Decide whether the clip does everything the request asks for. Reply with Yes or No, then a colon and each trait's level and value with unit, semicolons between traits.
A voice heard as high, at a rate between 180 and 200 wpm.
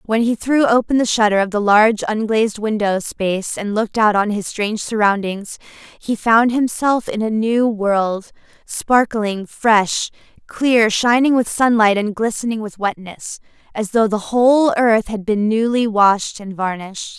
No: high, 220 Hz; average, 165 wpm